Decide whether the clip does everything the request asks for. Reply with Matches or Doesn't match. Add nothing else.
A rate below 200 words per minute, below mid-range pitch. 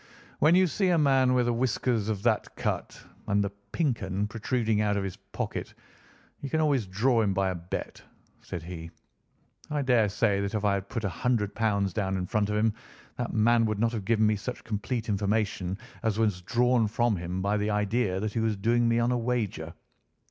Doesn't match